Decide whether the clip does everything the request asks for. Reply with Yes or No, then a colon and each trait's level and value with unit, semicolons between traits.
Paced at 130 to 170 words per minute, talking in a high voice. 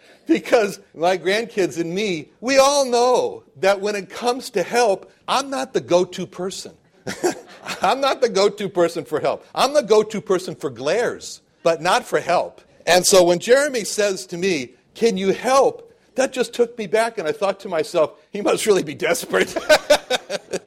No: average, 185 wpm; high, 205 Hz